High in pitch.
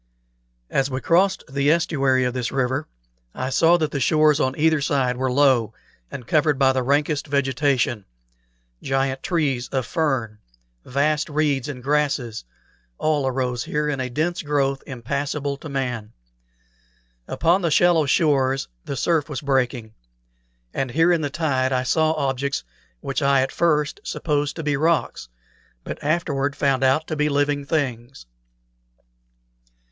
No: medium, 140 Hz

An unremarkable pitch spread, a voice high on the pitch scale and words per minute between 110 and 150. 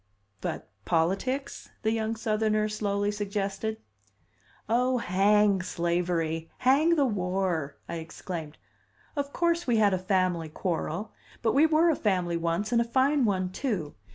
Yes: average, 4.8 semitones; high, 205 Hz; average, 140 wpm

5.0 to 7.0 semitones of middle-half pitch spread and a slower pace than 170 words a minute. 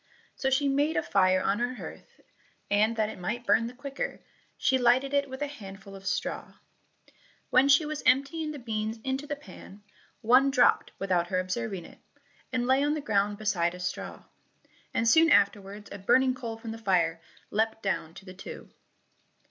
No: wide, 5.4 semitones; average, 185 wpm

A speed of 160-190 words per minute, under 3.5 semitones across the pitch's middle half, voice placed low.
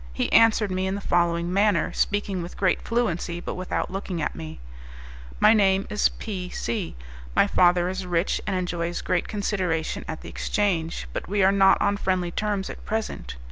No: average, 180 wpm; average, 2.7 semitones; medium, 185 Hz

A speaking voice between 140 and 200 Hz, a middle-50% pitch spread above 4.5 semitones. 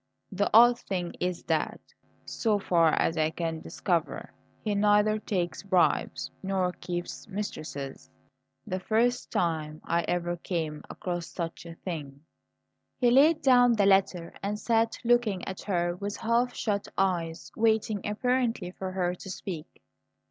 No: high, 190 Hz; average, 4.0 semitones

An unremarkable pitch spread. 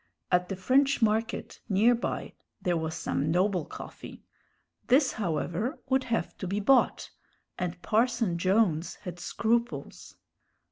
Yes: average, 4.9 semitones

